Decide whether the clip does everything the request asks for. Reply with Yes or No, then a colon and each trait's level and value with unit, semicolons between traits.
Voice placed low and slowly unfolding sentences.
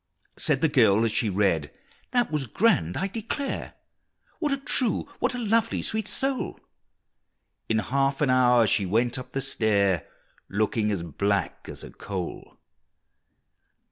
No: low, 125 Hz; average, 145 wpm